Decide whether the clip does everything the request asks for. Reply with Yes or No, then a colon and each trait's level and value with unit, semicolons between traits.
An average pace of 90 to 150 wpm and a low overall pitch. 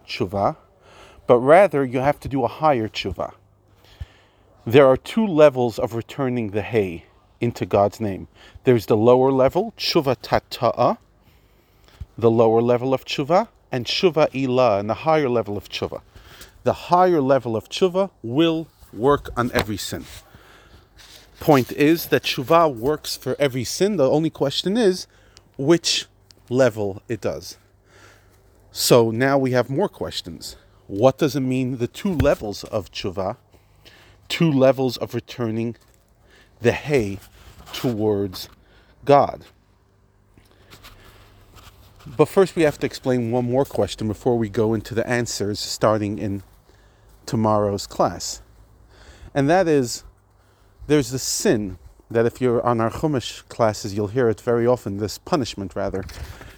Yes: average, 140 wpm; low, 115 Hz